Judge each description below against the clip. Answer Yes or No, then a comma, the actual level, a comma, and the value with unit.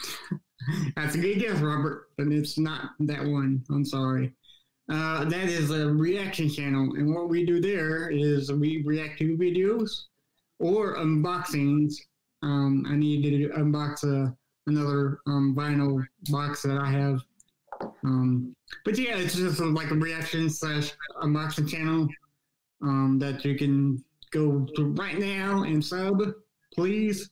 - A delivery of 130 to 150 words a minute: Yes, average, 145 wpm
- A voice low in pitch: No, medium, 150 Hz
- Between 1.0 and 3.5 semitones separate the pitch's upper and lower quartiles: Yes, narrow, 2.4 semitones